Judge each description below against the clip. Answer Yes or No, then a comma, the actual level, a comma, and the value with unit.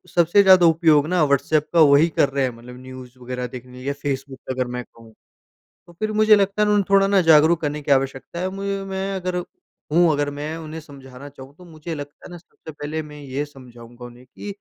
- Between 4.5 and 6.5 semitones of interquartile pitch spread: Yes, average, 4.8 semitones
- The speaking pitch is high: No, medium, 150 Hz